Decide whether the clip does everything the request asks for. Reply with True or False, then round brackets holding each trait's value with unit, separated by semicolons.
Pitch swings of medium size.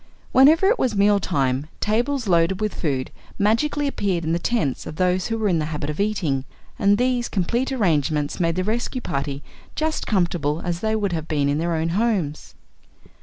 False (6.3 semitones)